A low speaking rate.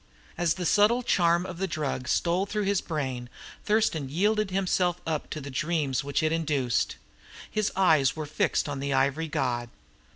No: average, 170 wpm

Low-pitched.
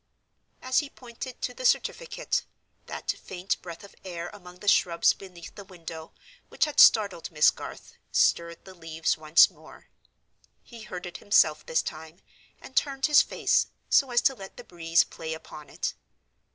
No: medium, 180 Hz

